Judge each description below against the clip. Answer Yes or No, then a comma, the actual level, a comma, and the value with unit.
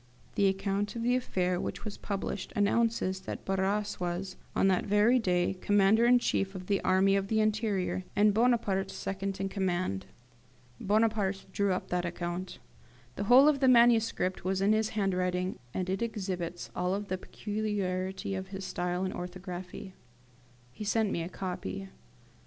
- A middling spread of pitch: No, narrow, 2.3 semitones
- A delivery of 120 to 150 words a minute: No, average, 160 wpm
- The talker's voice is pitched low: No, high, 195 Hz